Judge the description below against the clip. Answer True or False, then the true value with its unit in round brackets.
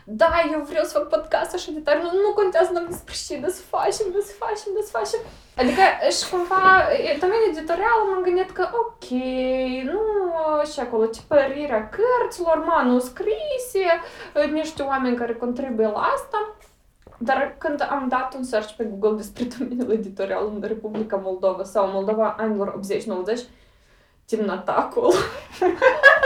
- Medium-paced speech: True (140 wpm)